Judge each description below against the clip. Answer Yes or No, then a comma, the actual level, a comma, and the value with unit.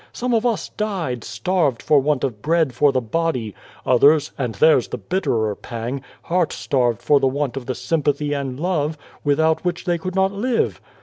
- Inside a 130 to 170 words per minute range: No, average, 185 wpm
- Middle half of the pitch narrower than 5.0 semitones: No, average, 5.3 semitones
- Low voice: No, medium, 145 Hz